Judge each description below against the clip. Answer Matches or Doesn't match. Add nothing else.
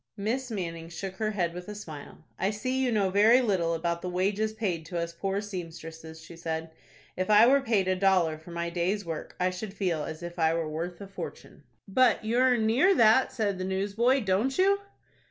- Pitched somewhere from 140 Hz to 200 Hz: Matches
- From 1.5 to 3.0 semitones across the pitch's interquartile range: Doesn't match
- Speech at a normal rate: Doesn't match